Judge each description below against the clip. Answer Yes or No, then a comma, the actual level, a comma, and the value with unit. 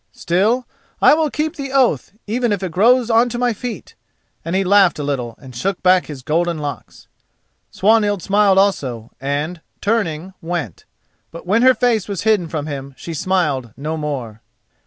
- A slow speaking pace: No, average, 175 wpm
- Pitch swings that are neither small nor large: No, wide, 6.7 semitones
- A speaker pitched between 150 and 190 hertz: Yes, medium, 185 Hz